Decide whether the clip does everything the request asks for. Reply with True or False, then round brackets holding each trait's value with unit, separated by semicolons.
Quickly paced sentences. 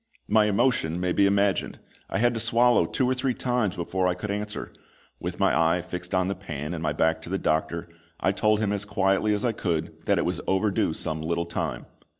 True (220 wpm)